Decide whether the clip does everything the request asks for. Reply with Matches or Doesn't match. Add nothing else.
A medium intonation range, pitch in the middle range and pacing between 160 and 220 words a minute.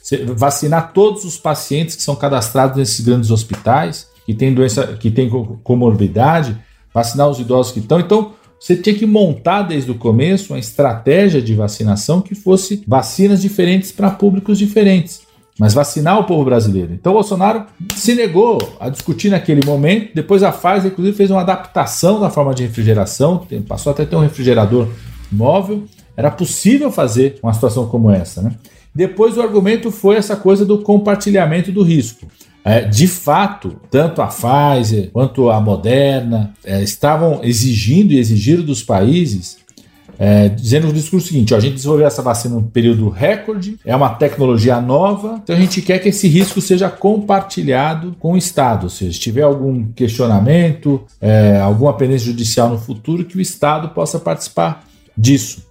Doesn't match